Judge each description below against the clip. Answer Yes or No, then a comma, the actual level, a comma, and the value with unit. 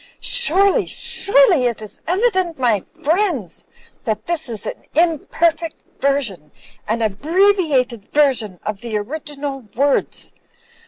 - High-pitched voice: Yes, very high, 280 Hz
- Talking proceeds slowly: Yes, slow, 115 wpm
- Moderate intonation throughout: No, wide, 7.2 semitones